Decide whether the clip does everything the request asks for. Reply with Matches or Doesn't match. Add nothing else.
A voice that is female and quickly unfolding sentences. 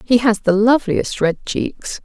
Doesn't match